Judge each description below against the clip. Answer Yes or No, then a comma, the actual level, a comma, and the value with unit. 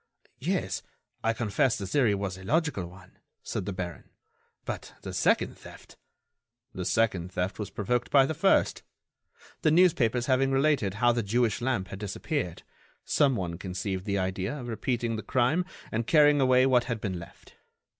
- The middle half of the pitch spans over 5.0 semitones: Yes, wide, 5.5 semitones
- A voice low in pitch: Yes, low, 115 Hz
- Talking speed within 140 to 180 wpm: Yes, average, 165 wpm